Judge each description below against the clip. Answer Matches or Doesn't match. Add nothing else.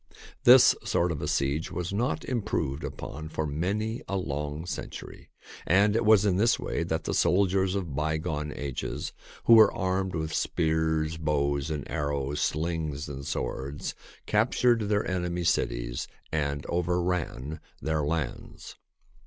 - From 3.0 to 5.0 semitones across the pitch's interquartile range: Matches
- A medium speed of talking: Matches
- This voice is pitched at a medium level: Doesn't match